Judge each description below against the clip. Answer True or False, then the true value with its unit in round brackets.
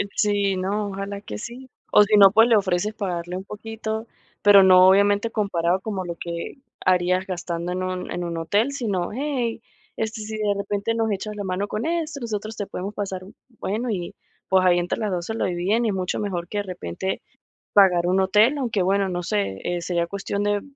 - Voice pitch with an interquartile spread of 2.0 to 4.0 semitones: True (2.9 semitones)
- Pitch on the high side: True (200 Hz)